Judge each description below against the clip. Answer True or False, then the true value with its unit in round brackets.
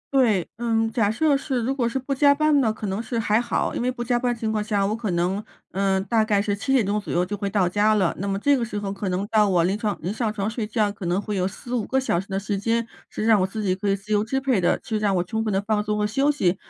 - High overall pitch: True (210 Hz)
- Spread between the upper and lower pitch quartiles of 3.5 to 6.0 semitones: False (3.0 semitones)